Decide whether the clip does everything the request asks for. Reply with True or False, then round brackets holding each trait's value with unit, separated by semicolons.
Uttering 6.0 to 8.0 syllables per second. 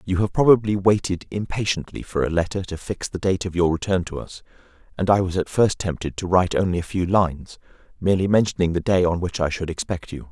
True (6.1 syllables/s)